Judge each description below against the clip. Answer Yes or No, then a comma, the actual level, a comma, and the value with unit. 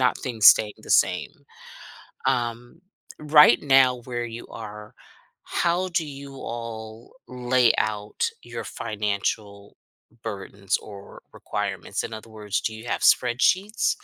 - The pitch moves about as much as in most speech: Yes, average, 3.5 semitones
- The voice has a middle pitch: No, low, 115 Hz